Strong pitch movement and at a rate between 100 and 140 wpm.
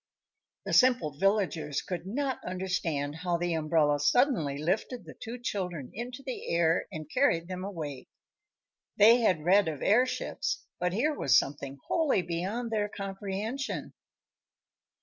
Yes: wide, 6.4 semitones; slow, 135 wpm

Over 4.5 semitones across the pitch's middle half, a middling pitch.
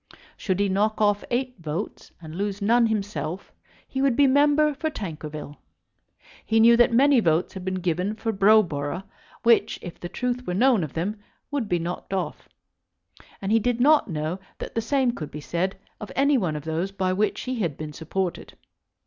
No: wide, 5.6 semitones; high, 200 Hz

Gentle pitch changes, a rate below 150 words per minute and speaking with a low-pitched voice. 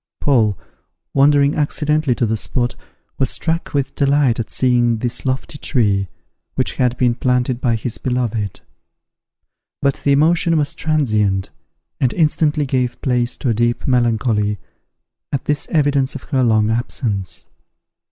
No: average, 3.5 semitones; average, 140 wpm; low, 125 Hz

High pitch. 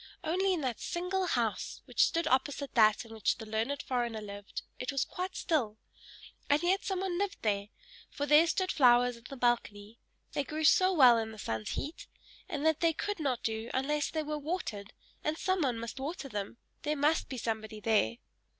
Yes: very high, 275 Hz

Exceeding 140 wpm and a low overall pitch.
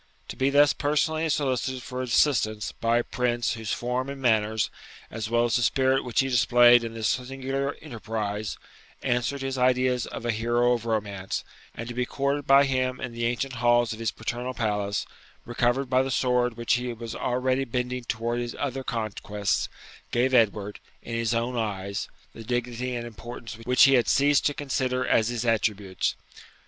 Yes: average, 175 wpm; low, 120 Hz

